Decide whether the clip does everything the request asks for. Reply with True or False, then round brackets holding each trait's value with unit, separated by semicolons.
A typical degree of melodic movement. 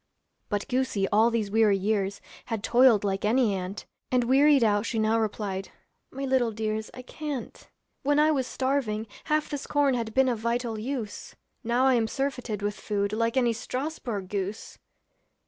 True (3.8 semitones)